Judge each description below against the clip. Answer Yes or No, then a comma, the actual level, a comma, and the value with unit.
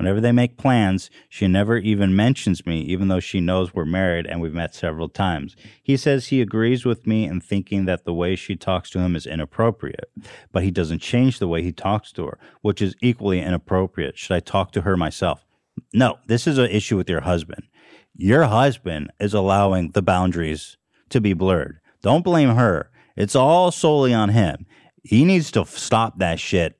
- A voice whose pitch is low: Yes, very low, 95 Hz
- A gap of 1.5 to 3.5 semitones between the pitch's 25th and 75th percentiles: No, average, 4.3 semitones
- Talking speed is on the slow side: No, average, 195 wpm